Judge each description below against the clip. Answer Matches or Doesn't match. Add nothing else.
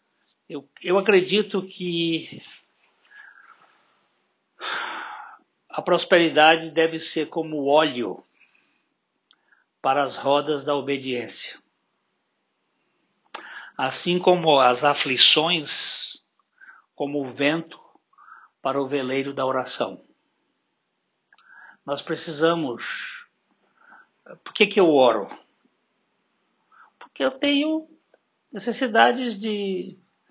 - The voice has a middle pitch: Matches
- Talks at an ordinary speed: Doesn't match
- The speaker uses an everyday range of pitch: Doesn't match